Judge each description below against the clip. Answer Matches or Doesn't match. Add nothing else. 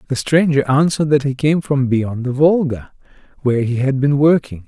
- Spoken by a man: Matches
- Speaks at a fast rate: Doesn't match